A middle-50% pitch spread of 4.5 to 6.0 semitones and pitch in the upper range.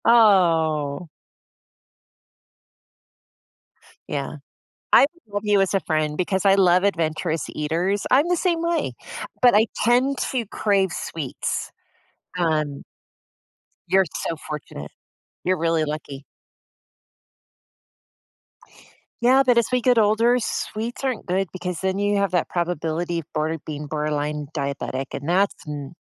No: wide, 5.4 semitones; medium, 180 Hz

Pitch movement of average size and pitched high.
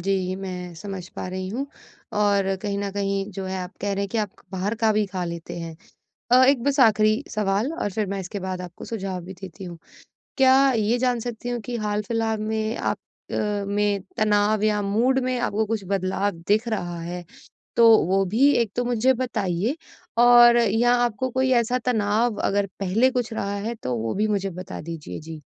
Yes: average, 3.4 semitones; high, 205 Hz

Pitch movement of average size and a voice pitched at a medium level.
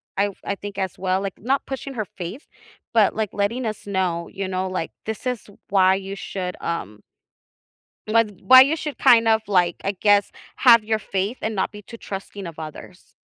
No: average, 3.1 semitones; high, 200 Hz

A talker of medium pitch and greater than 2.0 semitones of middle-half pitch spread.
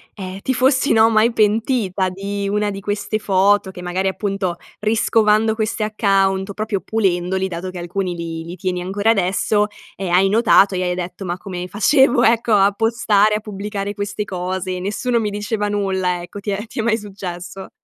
No: high, 200 Hz; narrow, 2.4 semitones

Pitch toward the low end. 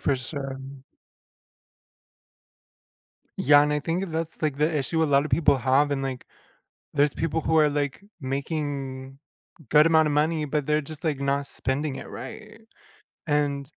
No: medium, 145 Hz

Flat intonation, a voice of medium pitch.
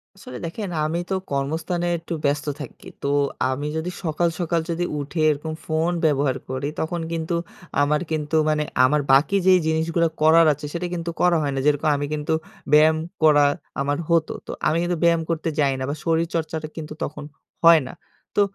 Yes: narrow, 2.3 semitones; medium, 160 Hz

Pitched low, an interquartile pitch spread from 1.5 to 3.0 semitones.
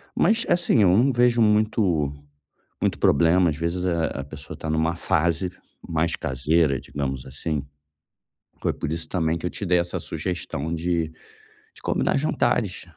Yes: very low, 85 Hz; average, 2.7 semitones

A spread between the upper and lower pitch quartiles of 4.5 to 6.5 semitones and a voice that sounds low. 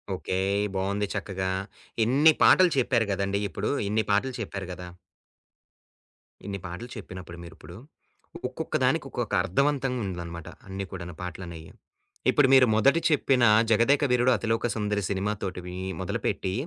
Yes: average, 4.8 semitones; low, 100 Hz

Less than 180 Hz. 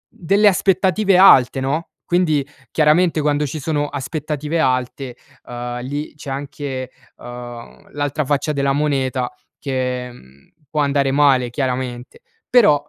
Yes: medium, 140 Hz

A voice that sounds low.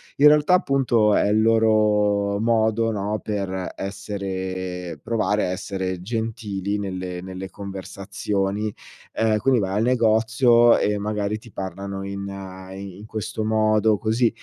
Yes: low, 105 Hz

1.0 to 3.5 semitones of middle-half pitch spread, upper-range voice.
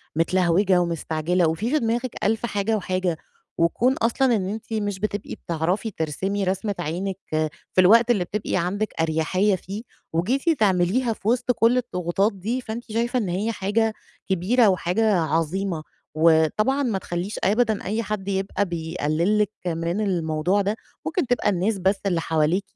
No: average, 4.1 semitones; high, 195 Hz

